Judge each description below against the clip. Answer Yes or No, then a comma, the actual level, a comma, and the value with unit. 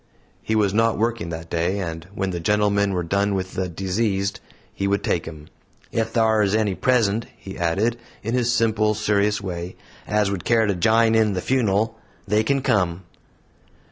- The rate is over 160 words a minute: Yes, average, 180 wpm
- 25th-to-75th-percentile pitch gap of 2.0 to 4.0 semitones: Yes, average, 3.0 semitones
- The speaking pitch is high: No, low, 100 Hz